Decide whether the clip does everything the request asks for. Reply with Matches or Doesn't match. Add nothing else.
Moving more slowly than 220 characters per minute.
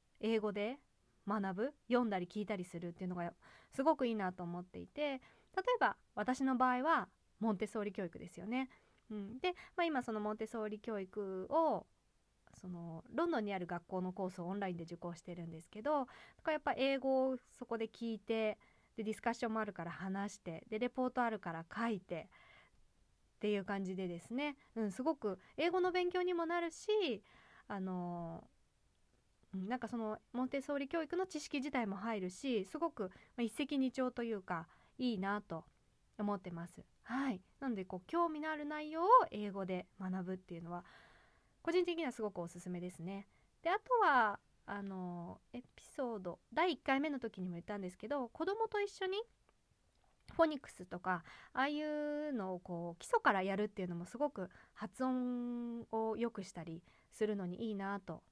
Doesn't match